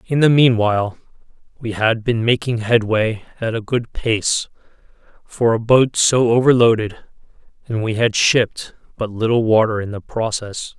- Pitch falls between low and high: No, low, 115 Hz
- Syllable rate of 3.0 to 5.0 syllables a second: Yes, 4.6 syllables/s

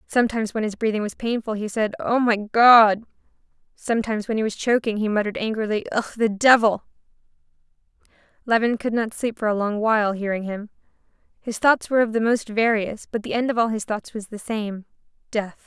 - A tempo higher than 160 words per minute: Yes, average, 190 wpm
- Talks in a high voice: Yes, high, 220 Hz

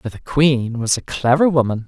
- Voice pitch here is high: No, low, 130 Hz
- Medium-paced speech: No, fast, 225 wpm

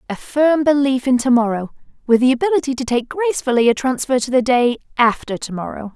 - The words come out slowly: No, average, 200 wpm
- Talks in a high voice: Yes, very high, 255 Hz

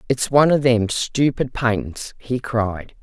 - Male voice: No, female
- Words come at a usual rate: Yes, average, 160 wpm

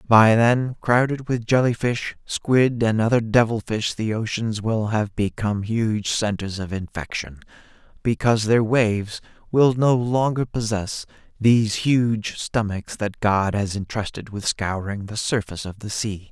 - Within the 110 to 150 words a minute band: Yes, average, 145 wpm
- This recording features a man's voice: Yes, male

